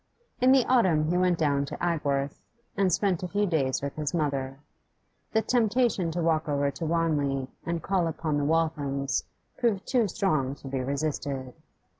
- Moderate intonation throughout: Yes, average, 4.5 semitones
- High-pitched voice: No, medium, 160 Hz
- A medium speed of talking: Yes, average, 170 wpm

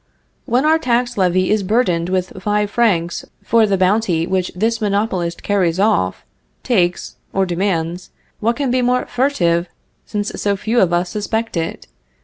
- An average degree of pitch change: Yes, average, 4.3 semitones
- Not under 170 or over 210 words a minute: No, average, 155 wpm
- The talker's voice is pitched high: Yes, high, 200 Hz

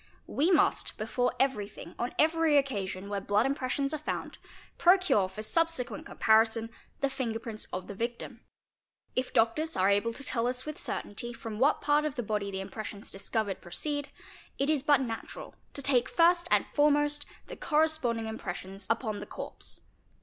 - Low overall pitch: No, high, 245 Hz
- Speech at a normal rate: Yes, average, 170 wpm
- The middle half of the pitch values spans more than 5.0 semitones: Yes, wide, 5.5 semitones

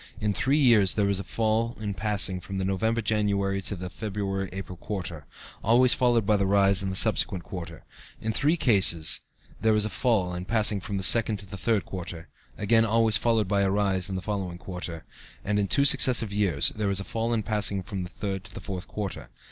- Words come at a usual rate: No, fast, 220 wpm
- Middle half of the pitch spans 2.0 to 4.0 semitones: Yes, narrow, 2.5 semitones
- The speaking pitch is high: No, low, 100 Hz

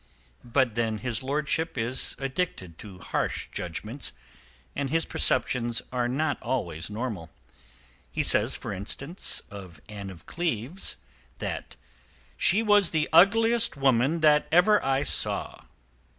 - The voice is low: Yes, low, 130 Hz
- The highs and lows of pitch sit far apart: Yes, wide, 7.1 semitones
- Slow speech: Yes, slow, 125 wpm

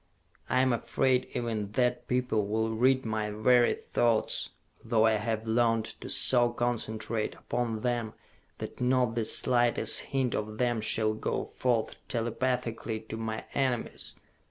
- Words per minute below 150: Yes, average, 140 wpm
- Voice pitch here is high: No, low, 115 Hz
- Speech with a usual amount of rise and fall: No, narrow, 2.0 semitones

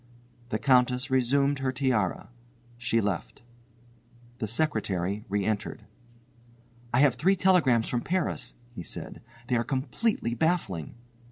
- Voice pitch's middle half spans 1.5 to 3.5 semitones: No, average, 4.4 semitones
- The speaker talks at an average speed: No, slow, 120 wpm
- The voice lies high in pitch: No, low, 125 Hz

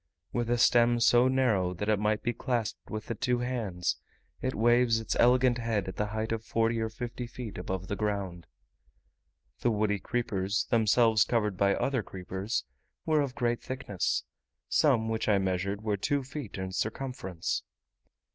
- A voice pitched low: Yes, low, 110 Hz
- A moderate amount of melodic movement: Yes, average, 3.3 semitones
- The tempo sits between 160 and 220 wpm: Yes, average, 165 wpm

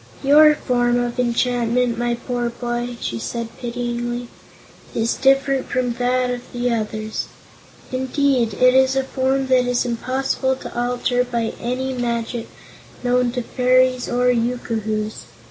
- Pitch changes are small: Yes, narrow, 1.3 semitones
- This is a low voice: No, high, 245 Hz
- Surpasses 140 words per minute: No, slow, 135 wpm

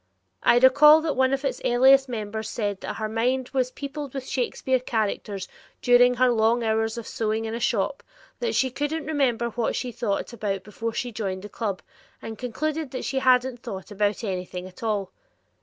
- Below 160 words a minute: No, average, 190 wpm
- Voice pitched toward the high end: Yes, high, 240 Hz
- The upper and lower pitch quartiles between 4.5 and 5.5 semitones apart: No, average, 3.4 semitones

